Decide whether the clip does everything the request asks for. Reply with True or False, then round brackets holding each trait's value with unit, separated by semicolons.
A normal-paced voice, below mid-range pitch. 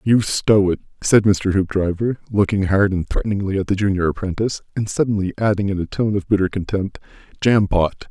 True (170 wpm; 100 Hz)